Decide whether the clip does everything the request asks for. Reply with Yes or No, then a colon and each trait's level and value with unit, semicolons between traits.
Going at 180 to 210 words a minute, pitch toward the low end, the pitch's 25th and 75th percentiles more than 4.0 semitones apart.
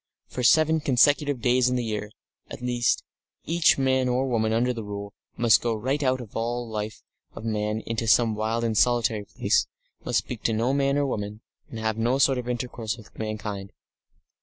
No: average, 195 wpm; low, 115 Hz; average, 2.7 semitones